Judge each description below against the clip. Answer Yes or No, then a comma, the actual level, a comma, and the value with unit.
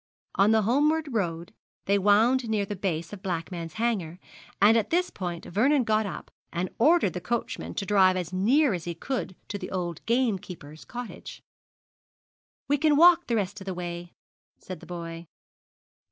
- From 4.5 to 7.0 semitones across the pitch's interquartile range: Yes, average, 5.3 semitones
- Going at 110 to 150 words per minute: No, average, 170 wpm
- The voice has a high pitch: Yes, high, 200 Hz